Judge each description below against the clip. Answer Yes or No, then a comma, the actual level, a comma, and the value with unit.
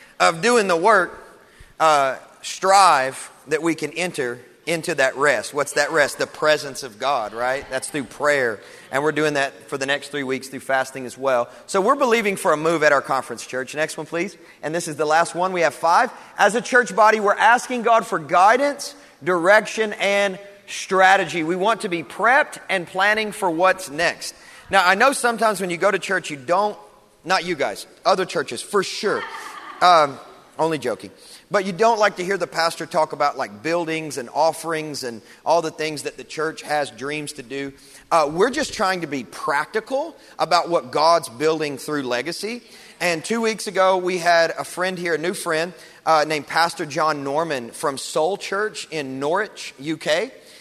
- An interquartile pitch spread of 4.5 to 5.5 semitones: Yes, average, 5.0 semitones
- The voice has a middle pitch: Yes, medium, 165 Hz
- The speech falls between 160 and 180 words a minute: No, average, 195 wpm